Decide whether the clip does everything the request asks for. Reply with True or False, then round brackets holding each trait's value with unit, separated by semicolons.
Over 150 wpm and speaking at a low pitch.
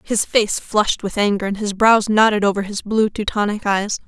False (205 wpm; 210 Hz)